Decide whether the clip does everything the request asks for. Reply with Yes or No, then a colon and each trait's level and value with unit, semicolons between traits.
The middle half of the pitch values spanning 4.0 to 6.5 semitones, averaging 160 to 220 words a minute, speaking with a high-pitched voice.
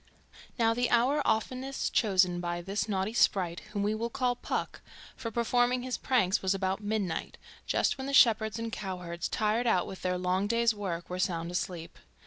Yes: average, 4.3 semitones; average, 180 wpm; high, 210 Hz